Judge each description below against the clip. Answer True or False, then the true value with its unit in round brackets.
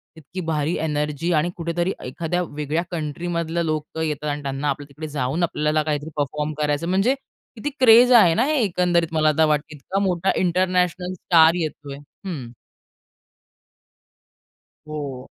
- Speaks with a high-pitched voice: False (160 Hz)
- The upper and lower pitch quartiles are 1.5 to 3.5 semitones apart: True (3.1 semitones)